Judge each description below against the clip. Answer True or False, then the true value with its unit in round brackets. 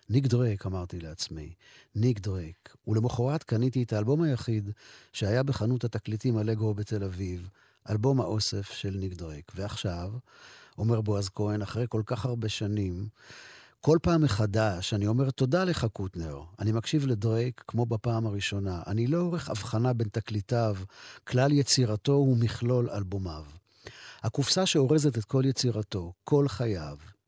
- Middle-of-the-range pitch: False (110 Hz)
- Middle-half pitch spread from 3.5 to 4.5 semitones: True (3.8 semitones)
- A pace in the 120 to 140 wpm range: True (135 wpm)